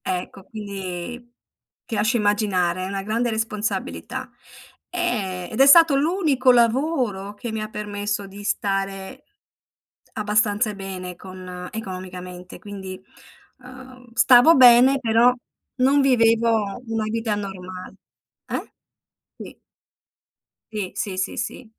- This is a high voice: Yes, high, 215 Hz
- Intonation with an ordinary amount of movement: Yes, average, 4.0 semitones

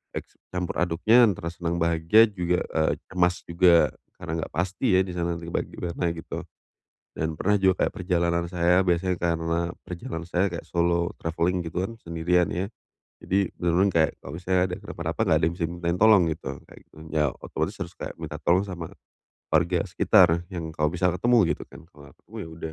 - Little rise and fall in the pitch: Yes, narrow, 1.6 semitones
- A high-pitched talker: No, very low, 85 Hz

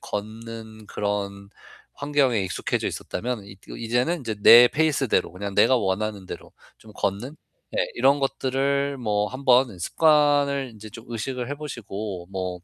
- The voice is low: Yes, low, 115 Hz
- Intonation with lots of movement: No, average, 4.9 semitones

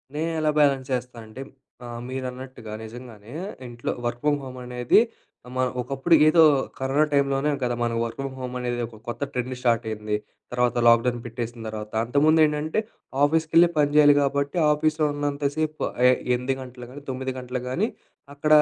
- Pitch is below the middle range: Yes, low, 130 Hz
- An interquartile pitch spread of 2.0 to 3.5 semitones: Yes, average, 3.2 semitones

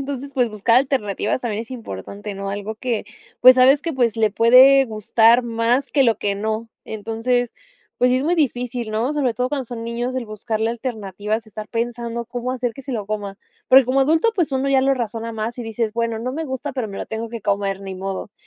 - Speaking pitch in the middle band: No, high, 235 Hz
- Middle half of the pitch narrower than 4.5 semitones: Yes, average, 3.0 semitones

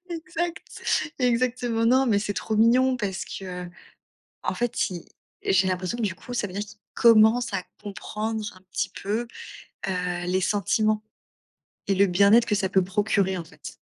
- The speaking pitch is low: No, high, 210 Hz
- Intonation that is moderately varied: Yes, average, 3.7 semitones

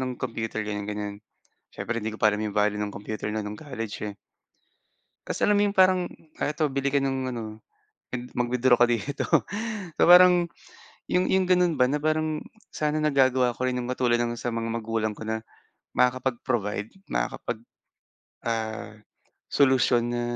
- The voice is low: Yes, low, 120 Hz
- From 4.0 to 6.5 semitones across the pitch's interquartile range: Yes, average, 4.3 semitones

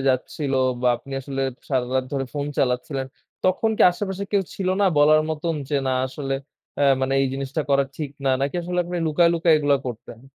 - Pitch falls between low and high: Yes, medium, 145 Hz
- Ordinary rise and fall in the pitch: Yes, average, 3.9 semitones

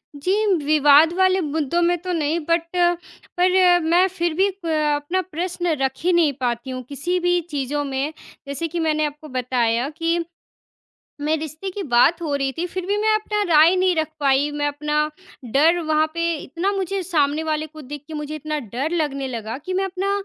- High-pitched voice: Yes, very high, 315 Hz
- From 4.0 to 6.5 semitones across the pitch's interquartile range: No, average, 3.4 semitones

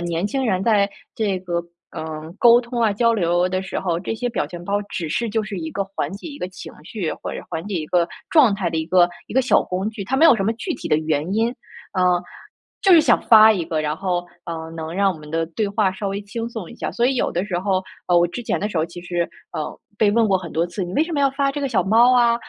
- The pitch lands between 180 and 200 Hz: Yes, high, 195 Hz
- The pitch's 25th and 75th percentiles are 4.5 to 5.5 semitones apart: Yes, average, 4.8 semitones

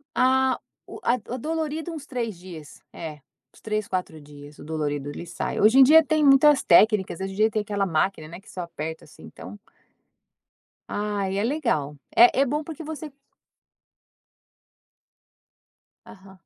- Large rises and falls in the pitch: Yes, wide, 8.2 semitones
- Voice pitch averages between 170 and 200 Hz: No, high, 210 Hz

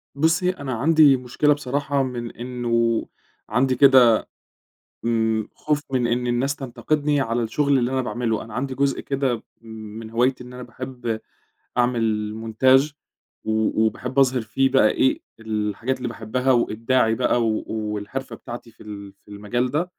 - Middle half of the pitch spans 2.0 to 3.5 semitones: Yes, average, 3.0 semitones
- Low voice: Yes, low, 125 Hz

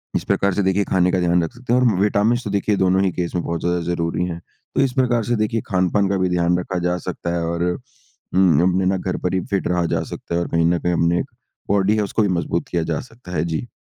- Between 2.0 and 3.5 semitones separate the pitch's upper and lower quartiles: Yes, average, 2.8 semitones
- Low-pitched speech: Yes, very low, 90 Hz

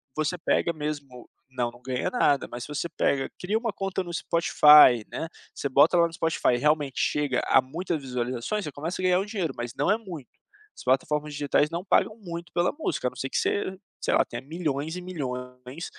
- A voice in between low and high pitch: Yes, medium, 150 Hz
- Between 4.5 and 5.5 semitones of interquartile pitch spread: Yes, average, 5.0 semitones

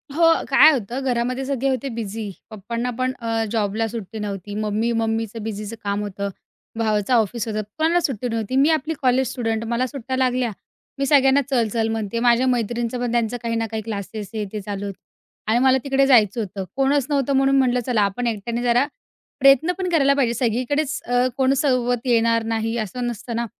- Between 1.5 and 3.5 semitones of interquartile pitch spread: Yes, average, 3.0 semitones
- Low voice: No, high, 235 Hz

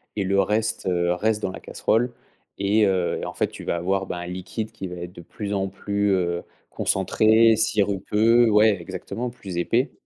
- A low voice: Yes, low, 100 Hz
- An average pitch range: Yes, average, 3.1 semitones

